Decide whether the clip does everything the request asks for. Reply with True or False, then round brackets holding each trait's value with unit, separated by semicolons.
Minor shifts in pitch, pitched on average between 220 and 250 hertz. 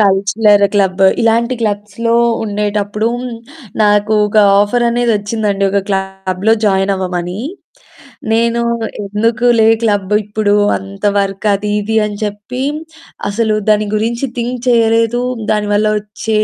False (2.1 semitones; 210 Hz)